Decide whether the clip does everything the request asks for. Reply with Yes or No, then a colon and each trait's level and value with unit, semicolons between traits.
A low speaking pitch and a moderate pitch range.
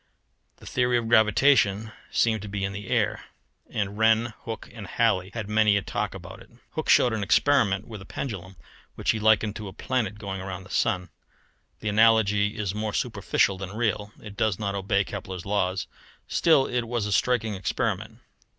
No: low, 105 Hz; narrow, 2.3 semitones